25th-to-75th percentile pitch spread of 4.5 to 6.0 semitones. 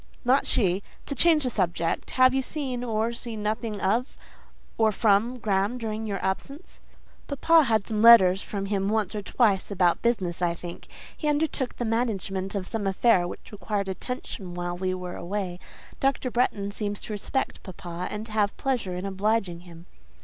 No: average, 4.0 semitones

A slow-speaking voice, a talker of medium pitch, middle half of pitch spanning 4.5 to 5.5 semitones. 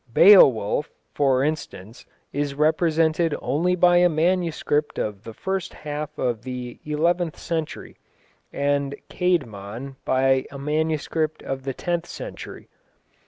No: slow, 120 wpm; medium, 150 Hz; average, 3.9 semitones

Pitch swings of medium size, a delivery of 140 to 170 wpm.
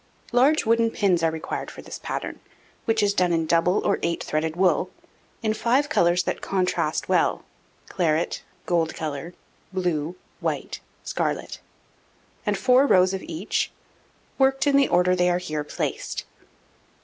Yes: average, 5.0 semitones; average, 150 wpm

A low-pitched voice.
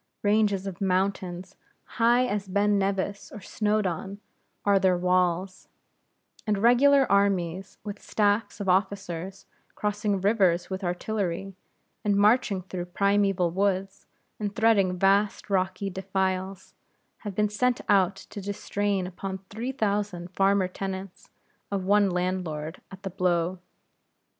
No: high, 195 Hz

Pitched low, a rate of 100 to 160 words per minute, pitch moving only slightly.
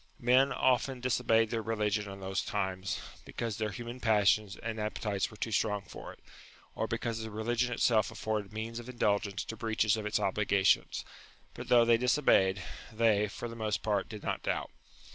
No: low, 110 Hz; average, 180 wpm; narrow, 2.3 semitones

